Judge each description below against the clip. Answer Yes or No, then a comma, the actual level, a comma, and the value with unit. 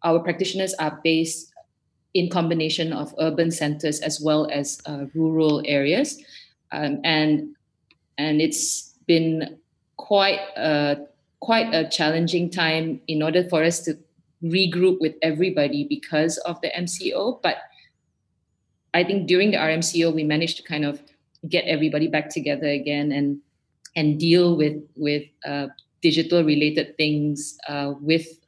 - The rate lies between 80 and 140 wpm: Yes, slow, 135 wpm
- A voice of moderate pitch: Yes, medium, 155 Hz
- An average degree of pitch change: No, narrow, 2.3 semitones